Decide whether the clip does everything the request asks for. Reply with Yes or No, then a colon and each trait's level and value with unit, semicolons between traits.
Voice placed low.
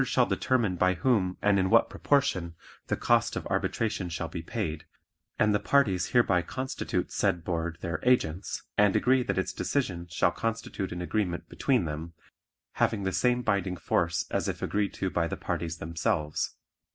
Yes: very low, 95 Hz